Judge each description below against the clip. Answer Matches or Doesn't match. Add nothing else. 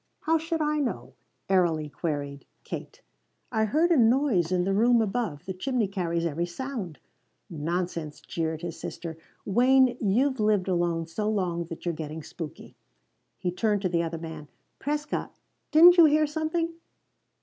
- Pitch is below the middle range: Doesn't match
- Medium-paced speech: Matches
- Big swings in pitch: Matches